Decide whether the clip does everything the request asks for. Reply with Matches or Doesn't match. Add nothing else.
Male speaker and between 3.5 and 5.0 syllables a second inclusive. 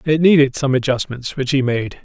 Doesn't match